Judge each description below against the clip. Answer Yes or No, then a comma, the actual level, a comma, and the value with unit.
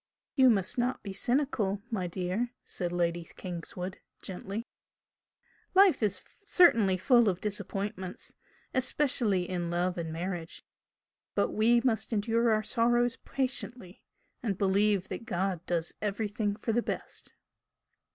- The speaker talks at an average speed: No, slow, 125 wpm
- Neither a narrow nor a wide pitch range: Yes, average, 4.5 semitones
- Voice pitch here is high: Yes, high, 205 Hz